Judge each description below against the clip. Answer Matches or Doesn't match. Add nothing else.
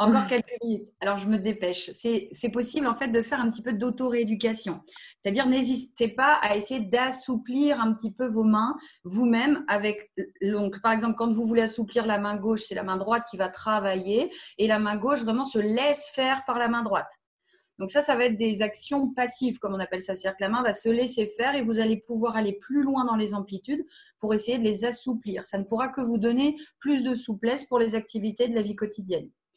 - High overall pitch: Matches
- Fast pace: Matches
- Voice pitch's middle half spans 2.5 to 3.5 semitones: Matches